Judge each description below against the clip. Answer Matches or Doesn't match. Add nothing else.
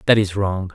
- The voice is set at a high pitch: Doesn't match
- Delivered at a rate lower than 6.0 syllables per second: Matches